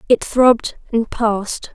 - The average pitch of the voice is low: No, high, 230 Hz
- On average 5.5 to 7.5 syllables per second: No, 4.3 syllables/s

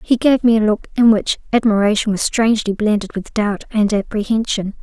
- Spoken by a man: No, female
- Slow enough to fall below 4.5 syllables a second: No, 5.5 syllables/s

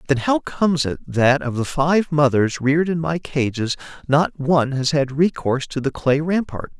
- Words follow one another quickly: No, average, 195 wpm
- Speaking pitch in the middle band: Yes, medium, 145 Hz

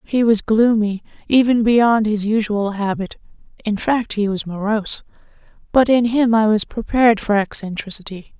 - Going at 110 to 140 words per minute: Yes, slow, 135 wpm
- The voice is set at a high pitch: Yes, high, 215 Hz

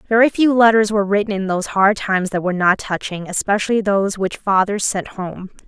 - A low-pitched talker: No, high, 200 Hz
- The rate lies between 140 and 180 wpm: No, average, 200 wpm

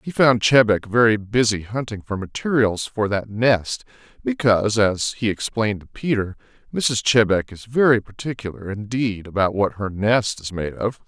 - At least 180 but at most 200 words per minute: No, average, 165 wpm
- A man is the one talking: Yes, male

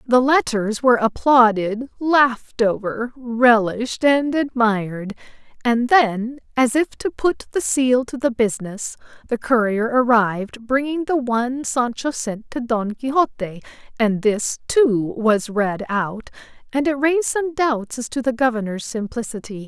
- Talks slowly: No, average, 145 wpm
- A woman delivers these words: Yes, female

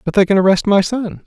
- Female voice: No, male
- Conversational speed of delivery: No, fast, 285 wpm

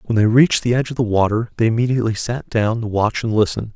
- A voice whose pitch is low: Yes, low, 115 Hz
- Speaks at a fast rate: Yes, fast, 255 wpm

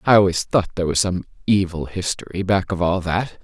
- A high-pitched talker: No, very low, 95 Hz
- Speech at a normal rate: No, fast, 210 wpm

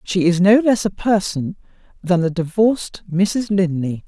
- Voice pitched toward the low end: No, high, 190 Hz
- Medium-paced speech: Yes, average, 160 wpm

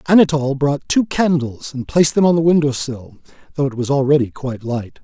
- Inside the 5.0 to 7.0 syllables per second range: Yes, 6.0 syllables/s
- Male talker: Yes, male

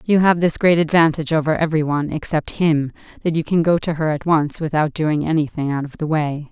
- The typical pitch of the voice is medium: Yes, medium, 155 Hz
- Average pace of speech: No, fast, 230 wpm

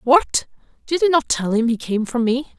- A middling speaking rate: No, fast, 230 wpm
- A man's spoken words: No, female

